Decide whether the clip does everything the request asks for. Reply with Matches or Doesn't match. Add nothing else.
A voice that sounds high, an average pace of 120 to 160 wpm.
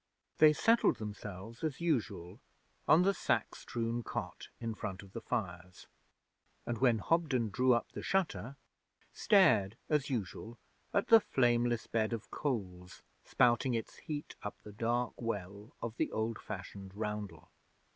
Doesn't match